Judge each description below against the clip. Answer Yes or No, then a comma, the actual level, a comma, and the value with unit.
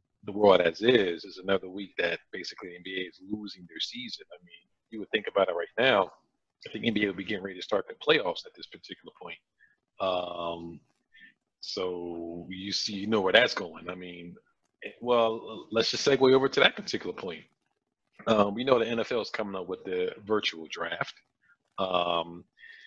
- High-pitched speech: No, low, 100 Hz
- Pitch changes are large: Yes, wide, 6.5 semitones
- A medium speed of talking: Yes, average, 190 wpm